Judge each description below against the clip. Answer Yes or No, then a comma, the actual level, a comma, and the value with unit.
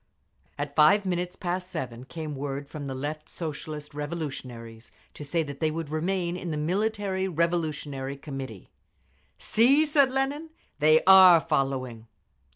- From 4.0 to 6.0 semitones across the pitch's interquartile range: Yes, average, 4.5 semitones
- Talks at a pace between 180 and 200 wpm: No, average, 140 wpm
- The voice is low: No, medium, 155 Hz